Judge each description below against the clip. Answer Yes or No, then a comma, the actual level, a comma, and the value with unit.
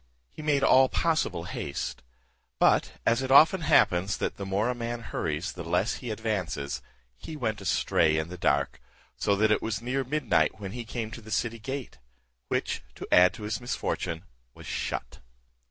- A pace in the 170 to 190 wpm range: Yes, average, 180 wpm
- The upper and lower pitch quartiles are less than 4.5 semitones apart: No, wide, 5.6 semitones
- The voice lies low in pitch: Yes, low, 110 Hz